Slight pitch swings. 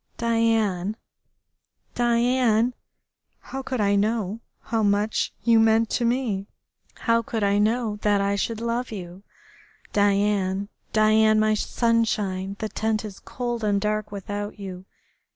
Yes: narrow, 2.3 semitones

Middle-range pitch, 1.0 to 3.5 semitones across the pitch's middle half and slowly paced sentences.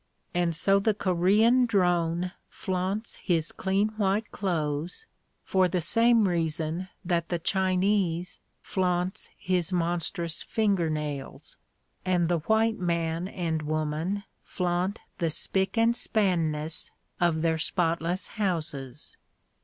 Yes: medium, 180 Hz; average, 3.0 semitones; slow, 115 wpm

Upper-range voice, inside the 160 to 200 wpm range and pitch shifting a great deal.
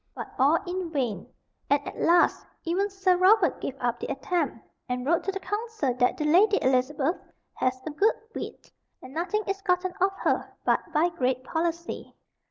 Yes: very high, 335 Hz; average, 180 wpm; wide, 5.7 semitones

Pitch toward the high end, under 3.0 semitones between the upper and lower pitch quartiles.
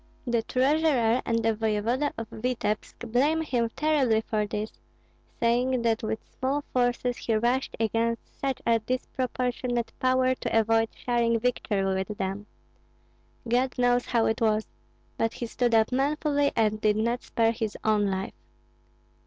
Yes: high, 235 Hz; narrow, 2.4 semitones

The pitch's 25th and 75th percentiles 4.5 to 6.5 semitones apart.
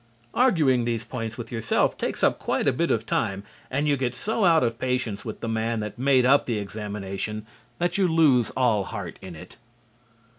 No: average, 4.1 semitones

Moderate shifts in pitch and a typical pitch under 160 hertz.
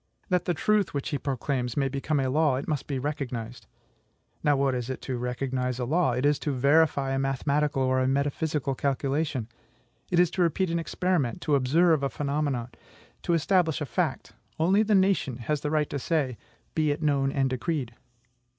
Yes: average, 3.3 semitones; medium, 140 Hz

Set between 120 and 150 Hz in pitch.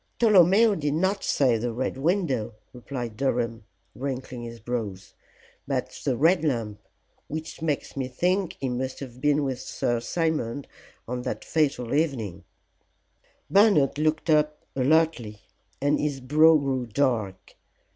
Yes: low, 135 Hz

